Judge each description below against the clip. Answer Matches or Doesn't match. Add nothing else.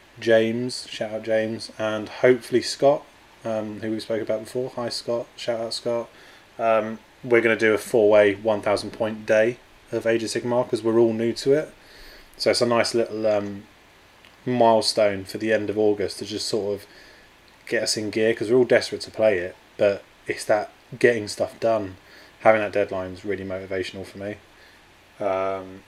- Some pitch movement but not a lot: Doesn't match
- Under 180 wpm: Doesn't match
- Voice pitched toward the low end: Matches